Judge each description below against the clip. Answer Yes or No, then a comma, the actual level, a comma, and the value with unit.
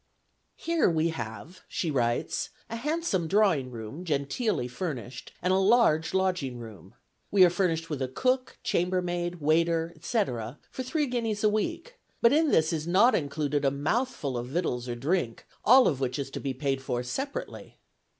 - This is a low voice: No, medium, 165 Hz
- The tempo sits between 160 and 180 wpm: Yes, average, 170 wpm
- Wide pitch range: Yes, wide, 7.8 semitones